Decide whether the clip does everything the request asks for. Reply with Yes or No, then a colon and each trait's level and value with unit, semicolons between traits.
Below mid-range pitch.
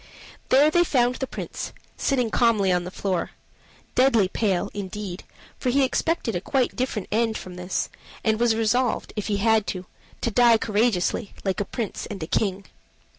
No: high, 220 Hz